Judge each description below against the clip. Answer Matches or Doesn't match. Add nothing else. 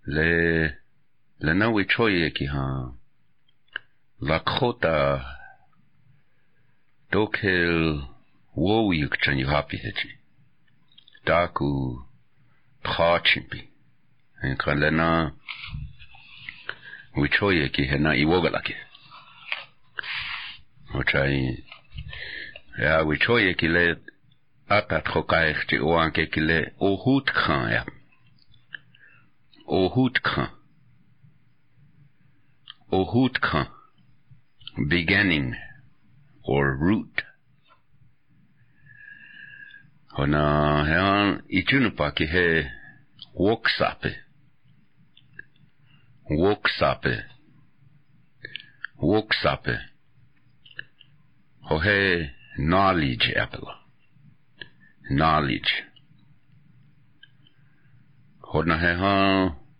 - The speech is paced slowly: Matches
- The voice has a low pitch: Matches